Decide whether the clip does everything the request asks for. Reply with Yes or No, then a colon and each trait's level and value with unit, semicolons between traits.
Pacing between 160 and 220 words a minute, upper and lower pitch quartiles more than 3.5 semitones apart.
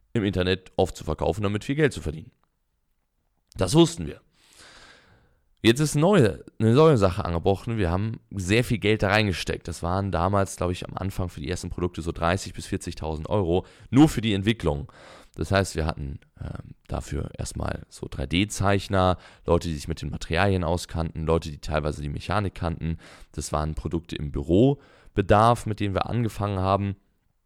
Yes: average, 175 wpm; average, 4.3 semitones